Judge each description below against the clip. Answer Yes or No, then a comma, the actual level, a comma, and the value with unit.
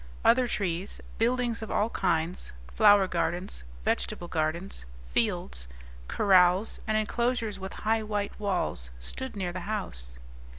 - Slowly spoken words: Yes, slow, 125 wpm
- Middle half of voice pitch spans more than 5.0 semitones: No, average, 4.2 semitones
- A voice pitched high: Yes, high, 195 Hz